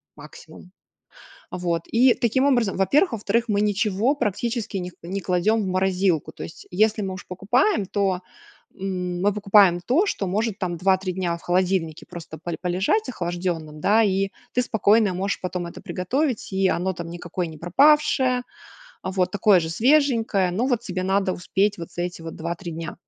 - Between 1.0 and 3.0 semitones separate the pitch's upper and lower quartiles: No, average, 3.7 semitones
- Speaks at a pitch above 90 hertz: Yes, high, 190 Hz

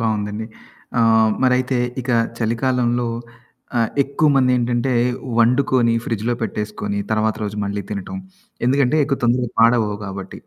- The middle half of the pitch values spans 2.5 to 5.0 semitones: Yes, average, 2.9 semitones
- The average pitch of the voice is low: Yes, low, 115 Hz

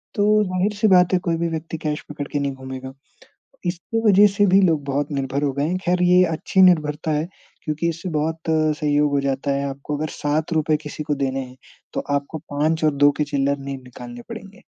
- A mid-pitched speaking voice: Yes, medium, 150 Hz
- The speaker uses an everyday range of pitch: Yes, average, 3.3 semitones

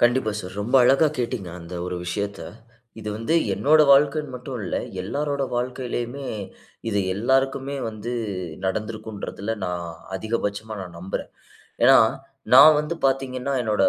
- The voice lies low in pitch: Yes, low, 120 Hz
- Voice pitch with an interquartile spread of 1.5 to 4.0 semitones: No, average, 4.7 semitones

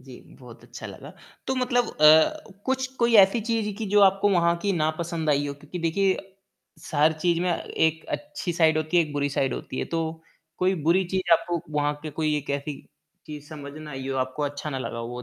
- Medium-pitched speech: Yes, medium, 160 Hz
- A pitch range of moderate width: Yes, average, 4.6 semitones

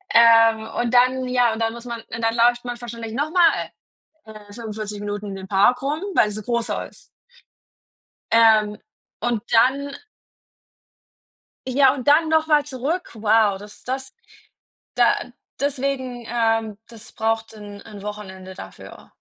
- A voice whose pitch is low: No, high, 230 Hz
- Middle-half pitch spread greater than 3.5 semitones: No, average, 3.2 semitones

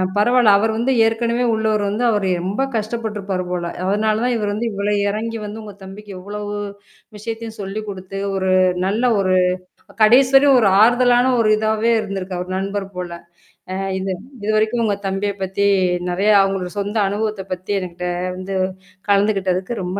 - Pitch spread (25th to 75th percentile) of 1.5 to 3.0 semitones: Yes, narrow, 2.5 semitones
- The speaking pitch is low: No, high, 205 Hz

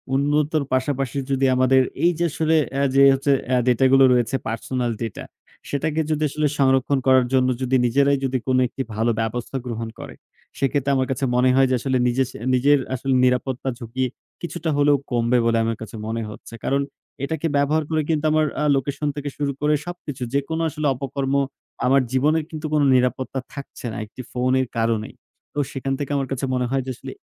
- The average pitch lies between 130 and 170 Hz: Yes, low, 135 Hz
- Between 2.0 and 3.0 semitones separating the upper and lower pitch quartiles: Yes, narrow, 2.4 semitones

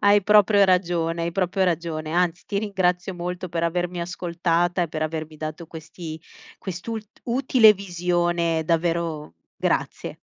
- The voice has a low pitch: No, medium, 175 Hz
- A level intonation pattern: Yes, narrow, 2.0 semitones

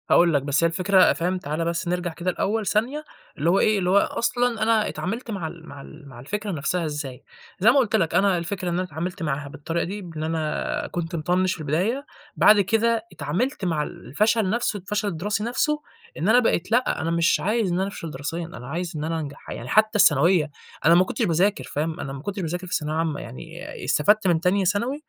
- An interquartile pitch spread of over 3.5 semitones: Yes, average, 4.4 semitones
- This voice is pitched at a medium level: Yes, medium, 180 Hz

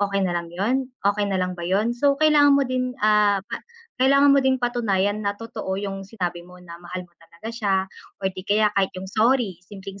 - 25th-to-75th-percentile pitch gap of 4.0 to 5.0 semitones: Yes, average, 4.4 semitones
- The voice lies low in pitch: No, high, 205 Hz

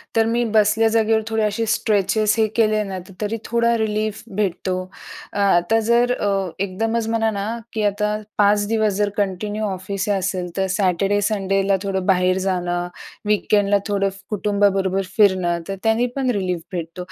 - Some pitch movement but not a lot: No, narrow, 2.3 semitones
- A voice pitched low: No, high, 205 Hz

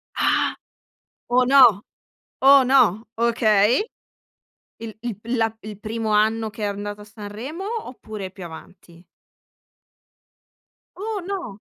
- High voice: Yes, high, 220 Hz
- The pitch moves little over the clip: No, average, 3.6 semitones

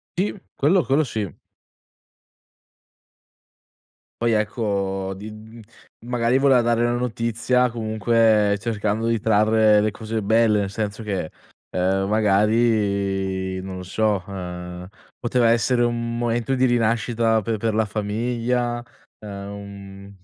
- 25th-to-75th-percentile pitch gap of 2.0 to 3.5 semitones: Yes, average, 2.7 semitones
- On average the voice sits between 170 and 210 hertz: No, low, 110 Hz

